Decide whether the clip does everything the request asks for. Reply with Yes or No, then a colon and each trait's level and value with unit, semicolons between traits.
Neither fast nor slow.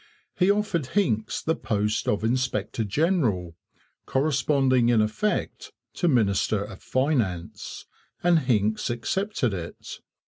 No: slow, 110 wpm